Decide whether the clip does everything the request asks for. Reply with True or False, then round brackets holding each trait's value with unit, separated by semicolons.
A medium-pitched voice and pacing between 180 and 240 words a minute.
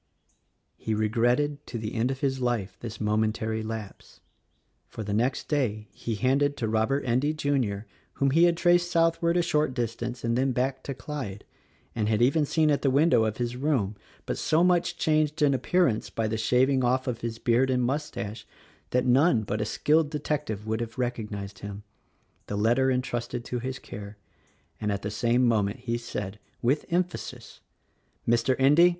False (125 Hz; 190 wpm)